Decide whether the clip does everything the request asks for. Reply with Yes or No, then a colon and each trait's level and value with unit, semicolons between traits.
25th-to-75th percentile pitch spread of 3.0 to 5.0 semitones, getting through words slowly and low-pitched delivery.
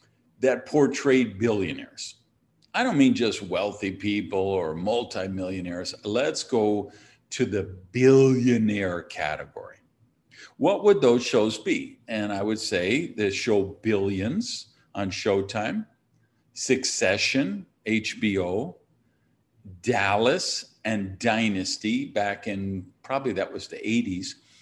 Yes: average, 4.5 semitones; slow, 105 wpm; low, 110 Hz